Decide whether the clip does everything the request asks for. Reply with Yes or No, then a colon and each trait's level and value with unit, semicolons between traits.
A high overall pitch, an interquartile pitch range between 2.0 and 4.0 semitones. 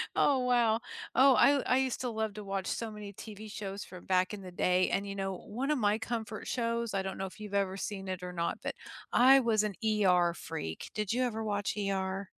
Yes: high, 205 Hz; average, 3.2 semitones